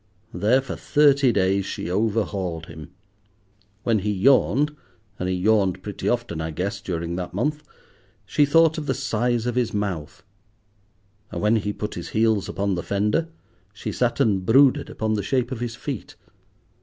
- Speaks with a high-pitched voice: No, low, 105 Hz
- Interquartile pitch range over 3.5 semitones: Yes, average, 5.0 semitones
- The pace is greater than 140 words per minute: Yes, average, 160 wpm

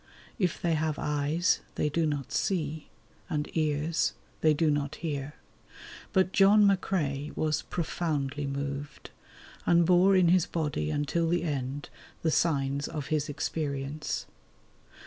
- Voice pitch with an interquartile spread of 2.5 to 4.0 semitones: Yes, average, 2.8 semitones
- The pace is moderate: No, slow, 130 wpm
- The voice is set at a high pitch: No, medium, 155 Hz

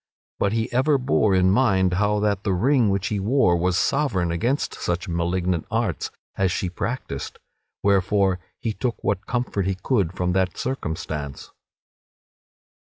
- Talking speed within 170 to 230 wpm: No, average, 150 wpm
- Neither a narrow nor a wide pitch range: Yes, average, 4.2 semitones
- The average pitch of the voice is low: Yes, very low, 95 Hz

